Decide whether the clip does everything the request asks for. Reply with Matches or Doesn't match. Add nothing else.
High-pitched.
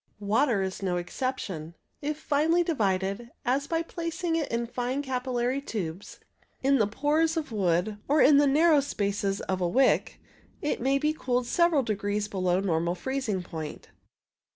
Matches